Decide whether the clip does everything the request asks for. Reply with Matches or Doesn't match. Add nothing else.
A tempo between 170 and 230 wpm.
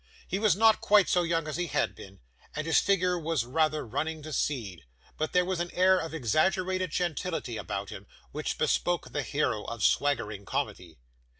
Matches